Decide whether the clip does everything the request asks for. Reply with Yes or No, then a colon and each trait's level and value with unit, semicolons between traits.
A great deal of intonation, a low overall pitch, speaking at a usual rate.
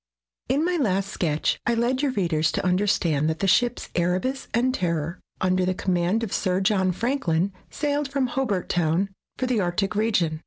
No: wide, 5.8 semitones; high, 195 Hz; average, 180 wpm